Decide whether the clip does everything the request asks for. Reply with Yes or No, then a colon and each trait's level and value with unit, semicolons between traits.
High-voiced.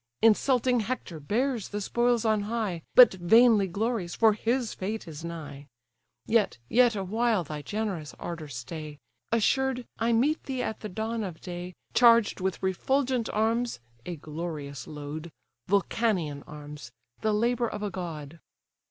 Yes: high, 205 Hz